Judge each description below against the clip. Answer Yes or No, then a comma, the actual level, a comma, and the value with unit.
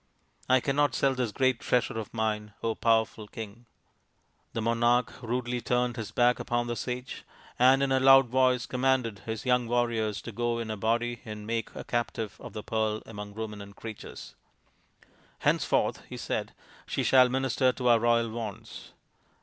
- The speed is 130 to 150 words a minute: No, average, 175 wpm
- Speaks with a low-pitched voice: Yes, low, 120 Hz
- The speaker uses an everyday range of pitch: No, narrow, 2.2 semitones